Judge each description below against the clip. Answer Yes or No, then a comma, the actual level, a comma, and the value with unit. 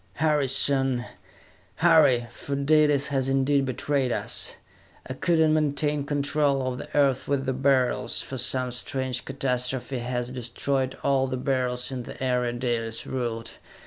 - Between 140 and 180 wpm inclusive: Yes, average, 145 wpm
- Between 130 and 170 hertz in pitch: Yes, low, 135 Hz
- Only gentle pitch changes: Yes, narrow, 2.1 semitones